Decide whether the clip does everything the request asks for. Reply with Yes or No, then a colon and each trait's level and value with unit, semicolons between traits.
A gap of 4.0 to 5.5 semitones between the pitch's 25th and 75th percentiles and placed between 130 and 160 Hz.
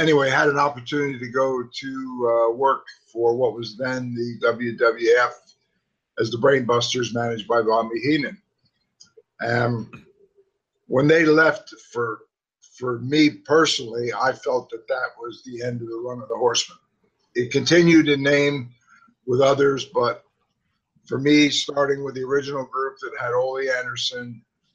Yes: average, 4.5 semitones; low, 135 Hz